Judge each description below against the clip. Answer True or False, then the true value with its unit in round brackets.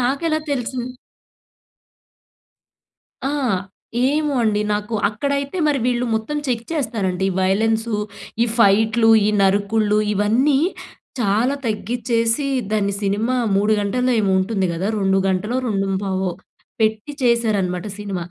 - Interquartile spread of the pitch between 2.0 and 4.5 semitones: True (3.9 semitones)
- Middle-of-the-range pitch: False (220 Hz)